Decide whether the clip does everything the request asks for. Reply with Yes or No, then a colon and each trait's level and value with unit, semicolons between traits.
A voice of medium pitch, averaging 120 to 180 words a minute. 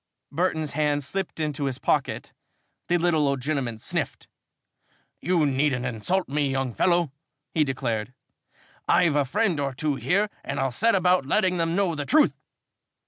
Yes: medium, 150 Hz; average, 155 wpm